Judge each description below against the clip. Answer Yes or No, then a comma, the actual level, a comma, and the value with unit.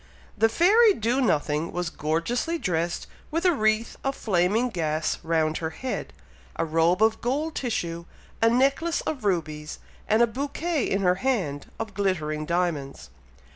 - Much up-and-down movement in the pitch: Yes, wide, 7.5 semitones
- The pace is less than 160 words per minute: Yes, average, 150 wpm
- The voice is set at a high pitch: Yes, high, 200 Hz